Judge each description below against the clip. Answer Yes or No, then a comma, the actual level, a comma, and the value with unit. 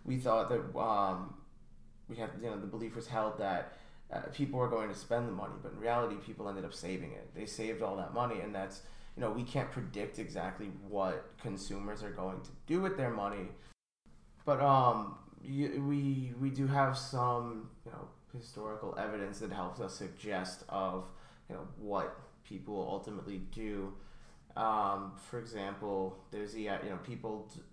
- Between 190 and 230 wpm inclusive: No, average, 175 wpm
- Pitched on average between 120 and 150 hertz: No, low, 110 Hz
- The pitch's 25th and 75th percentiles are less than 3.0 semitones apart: No, average, 3.8 semitones